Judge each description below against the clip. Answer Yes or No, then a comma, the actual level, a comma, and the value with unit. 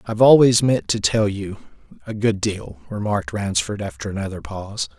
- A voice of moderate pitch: No, low, 105 Hz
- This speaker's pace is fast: No, average, 155 wpm